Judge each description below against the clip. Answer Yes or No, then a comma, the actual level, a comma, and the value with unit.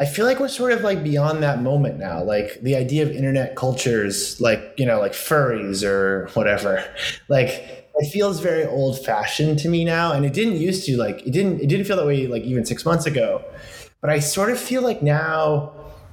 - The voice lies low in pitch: No, medium, 150 Hz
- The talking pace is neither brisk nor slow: No, fast, 215 wpm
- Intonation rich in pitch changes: Yes, wide, 5.8 semitones